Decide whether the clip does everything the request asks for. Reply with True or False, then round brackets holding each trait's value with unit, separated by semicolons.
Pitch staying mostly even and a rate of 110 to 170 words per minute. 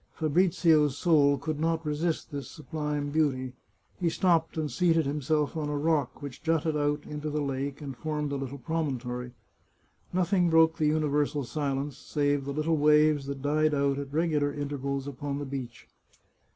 False (2.1 semitones; 180 wpm)